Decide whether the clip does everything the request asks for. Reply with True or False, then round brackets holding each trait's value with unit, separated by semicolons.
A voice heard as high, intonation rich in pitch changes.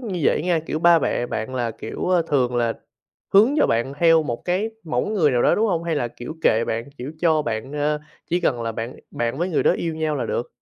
False (150 Hz; 6.1 semitones)